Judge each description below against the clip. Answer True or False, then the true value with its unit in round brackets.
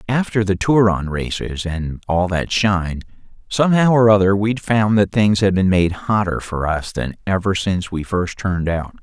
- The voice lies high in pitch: False (100 Hz)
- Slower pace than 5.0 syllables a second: True (4.7 syllables/s)